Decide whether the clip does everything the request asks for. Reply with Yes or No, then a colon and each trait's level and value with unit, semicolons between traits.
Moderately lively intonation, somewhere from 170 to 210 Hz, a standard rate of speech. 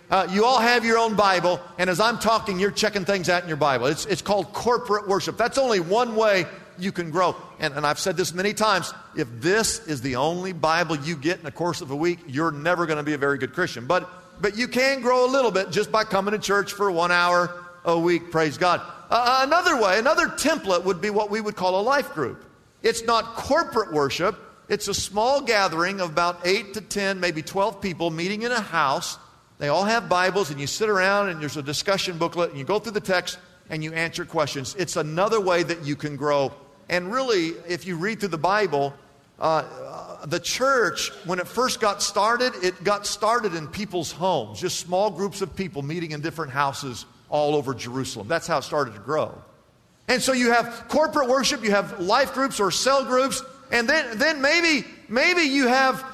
No: average, 4.9 semitones; high, 190 Hz; fast, 220 wpm